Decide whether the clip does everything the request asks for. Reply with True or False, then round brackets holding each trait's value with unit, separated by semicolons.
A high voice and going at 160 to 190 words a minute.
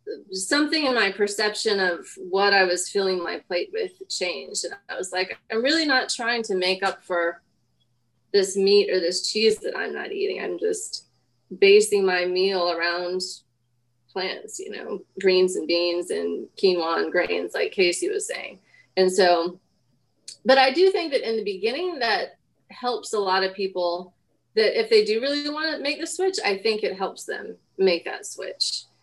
True (210 Hz; 180 wpm)